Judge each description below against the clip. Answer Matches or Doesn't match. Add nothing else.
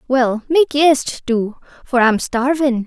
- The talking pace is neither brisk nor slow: Matches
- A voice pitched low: Doesn't match